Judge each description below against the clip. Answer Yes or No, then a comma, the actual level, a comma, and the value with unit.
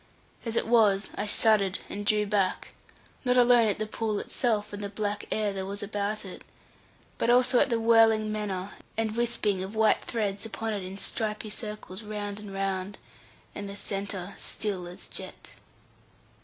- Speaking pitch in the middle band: No, high, 210 Hz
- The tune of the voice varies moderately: No, narrow, 1.8 semitones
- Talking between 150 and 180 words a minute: Yes, average, 170 wpm